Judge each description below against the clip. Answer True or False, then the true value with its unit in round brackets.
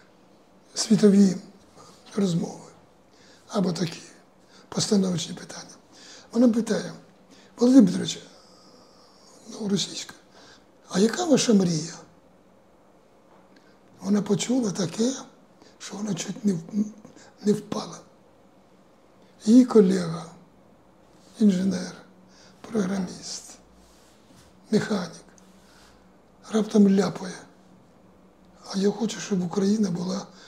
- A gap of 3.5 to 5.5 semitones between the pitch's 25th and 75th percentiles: False (2.7 semitones)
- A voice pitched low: False (200 Hz)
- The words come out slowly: True (75 wpm)